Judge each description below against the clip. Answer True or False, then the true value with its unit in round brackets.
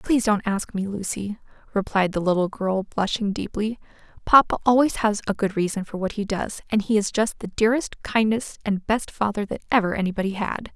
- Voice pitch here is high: True (205 Hz)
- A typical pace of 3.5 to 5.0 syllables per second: False (5.5 syllables/s)